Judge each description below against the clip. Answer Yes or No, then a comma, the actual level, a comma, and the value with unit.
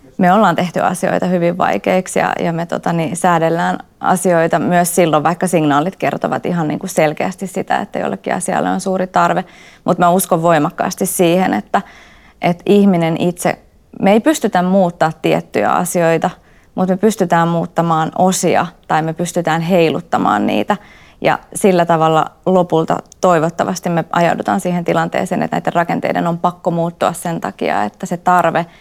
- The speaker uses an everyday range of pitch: No, narrow, 1.9 semitones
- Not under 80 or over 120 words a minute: No, fast, 155 wpm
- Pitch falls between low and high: Yes, medium, 175 Hz